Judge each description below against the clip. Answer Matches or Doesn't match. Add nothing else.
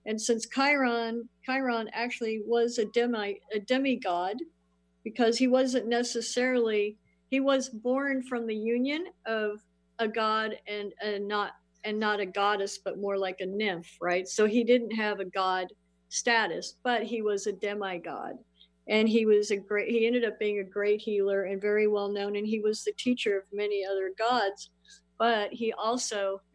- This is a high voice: Matches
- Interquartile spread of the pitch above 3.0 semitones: Doesn't match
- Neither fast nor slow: Matches